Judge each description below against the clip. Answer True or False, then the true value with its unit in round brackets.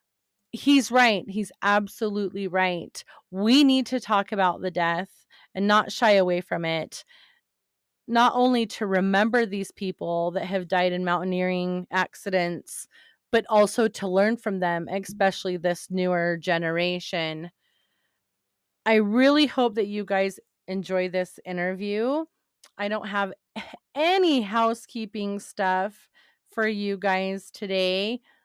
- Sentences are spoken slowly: True (125 wpm)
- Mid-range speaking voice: False (200 Hz)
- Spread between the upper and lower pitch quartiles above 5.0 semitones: False (3.4 semitones)